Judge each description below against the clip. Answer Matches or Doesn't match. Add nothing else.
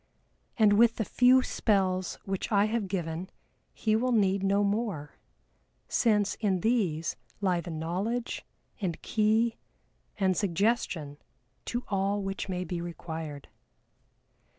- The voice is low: Doesn't match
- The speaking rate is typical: Doesn't match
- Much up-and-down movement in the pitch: Doesn't match